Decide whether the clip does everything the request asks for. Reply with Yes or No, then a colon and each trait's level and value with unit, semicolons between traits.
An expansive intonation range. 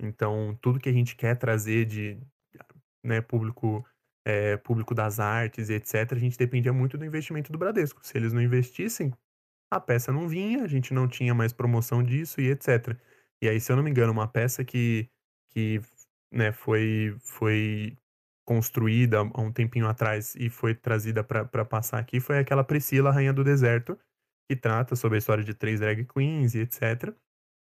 No: average, 2.9 semitones